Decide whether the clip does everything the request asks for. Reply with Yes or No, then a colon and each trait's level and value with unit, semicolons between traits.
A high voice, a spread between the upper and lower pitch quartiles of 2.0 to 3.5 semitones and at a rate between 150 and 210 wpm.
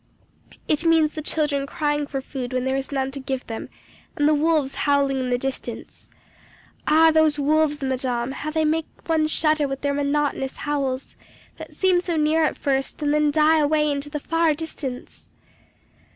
Yes: very high, 295 Hz; narrow, 2.4 semitones; average, 180 wpm